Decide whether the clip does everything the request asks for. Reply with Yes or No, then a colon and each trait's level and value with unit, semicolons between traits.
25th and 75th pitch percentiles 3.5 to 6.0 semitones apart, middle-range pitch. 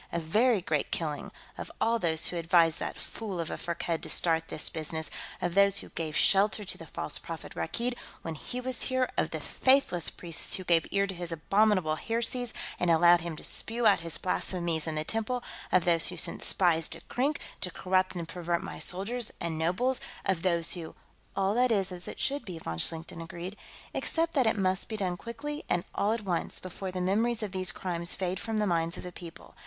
Yes: average, 4.4 semitones; medium, 180 Hz